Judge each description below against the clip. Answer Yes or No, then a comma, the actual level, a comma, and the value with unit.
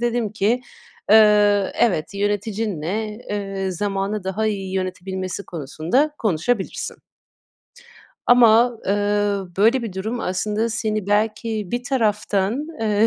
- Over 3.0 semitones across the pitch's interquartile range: No, narrow, 2.5 semitones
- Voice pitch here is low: No, high, 210 Hz